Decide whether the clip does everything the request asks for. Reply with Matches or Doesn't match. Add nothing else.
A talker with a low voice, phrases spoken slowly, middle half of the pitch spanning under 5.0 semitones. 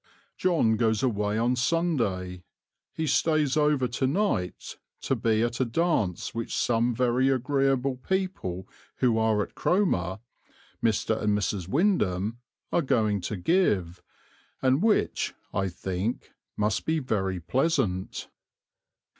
Doesn't match